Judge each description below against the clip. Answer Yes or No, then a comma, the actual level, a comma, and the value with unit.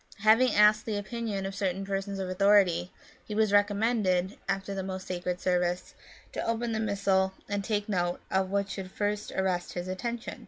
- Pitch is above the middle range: Yes, high, 195 Hz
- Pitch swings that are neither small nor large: No, narrow, 2.0 semitones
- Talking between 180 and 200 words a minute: Yes, average, 185 wpm